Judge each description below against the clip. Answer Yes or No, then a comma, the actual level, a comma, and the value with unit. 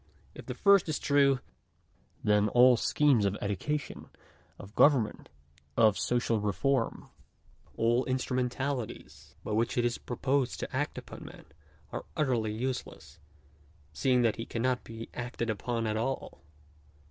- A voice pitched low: Yes, low, 120 Hz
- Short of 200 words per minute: Yes, slow, 135 wpm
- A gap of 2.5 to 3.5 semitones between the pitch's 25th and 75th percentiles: Yes, average, 3.1 semitones